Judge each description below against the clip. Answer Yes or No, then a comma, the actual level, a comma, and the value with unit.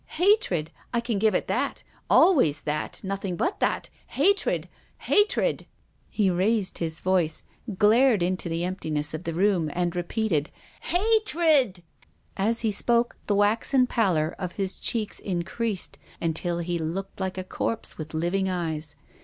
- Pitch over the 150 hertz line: Yes, high, 190 Hz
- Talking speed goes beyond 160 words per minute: Yes, average, 170 wpm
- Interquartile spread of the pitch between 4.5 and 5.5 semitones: Yes, average, 5.1 semitones